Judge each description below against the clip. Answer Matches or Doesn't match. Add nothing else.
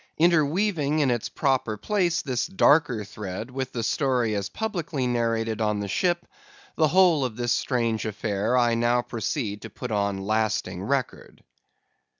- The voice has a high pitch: Doesn't match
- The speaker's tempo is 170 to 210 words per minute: Doesn't match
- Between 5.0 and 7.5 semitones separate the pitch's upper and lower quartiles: Matches